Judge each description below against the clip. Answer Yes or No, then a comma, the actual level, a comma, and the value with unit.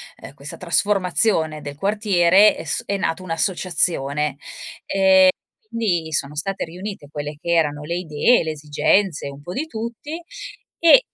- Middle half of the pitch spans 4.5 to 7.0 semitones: Yes, average, 5.1 semitones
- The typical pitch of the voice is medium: Yes, medium, 175 Hz